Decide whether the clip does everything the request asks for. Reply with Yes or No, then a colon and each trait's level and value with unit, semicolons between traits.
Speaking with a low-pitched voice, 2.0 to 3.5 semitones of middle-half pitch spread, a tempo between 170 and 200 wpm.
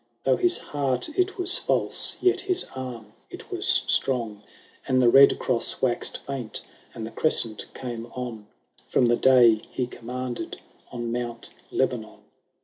No: low, 125 Hz; average, 2.7 semitones; average, 145 wpm